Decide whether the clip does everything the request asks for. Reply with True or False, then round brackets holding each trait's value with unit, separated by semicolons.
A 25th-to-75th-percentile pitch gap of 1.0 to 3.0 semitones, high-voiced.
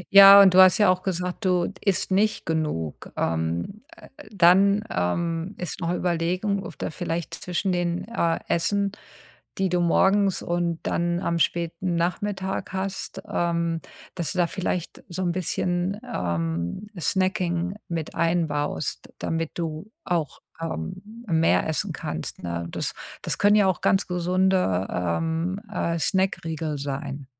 False (2.6 semitones; 175 Hz)